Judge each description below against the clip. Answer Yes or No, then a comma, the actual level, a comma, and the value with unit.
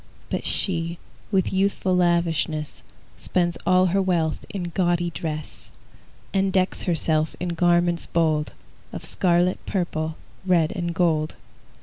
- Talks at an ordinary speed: No, slow, 120 wpm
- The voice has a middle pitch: Yes, medium, 175 Hz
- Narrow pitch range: Yes, narrow, 2.0 semitones